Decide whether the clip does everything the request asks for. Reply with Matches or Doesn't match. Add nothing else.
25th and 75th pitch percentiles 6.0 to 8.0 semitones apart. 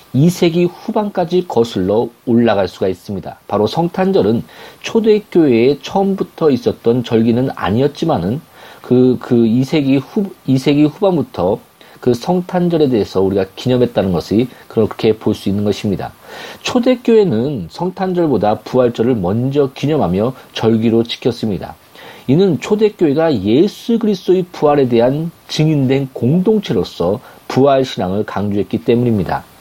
Matches